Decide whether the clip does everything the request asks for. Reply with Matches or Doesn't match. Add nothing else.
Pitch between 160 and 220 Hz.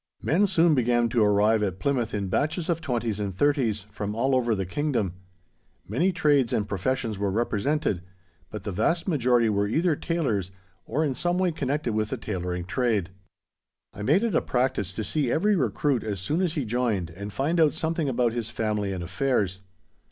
Doesn't match